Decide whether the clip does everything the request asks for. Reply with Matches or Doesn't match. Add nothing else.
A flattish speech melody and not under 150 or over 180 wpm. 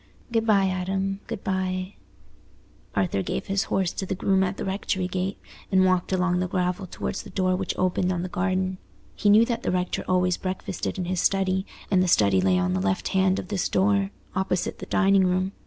Doesn't match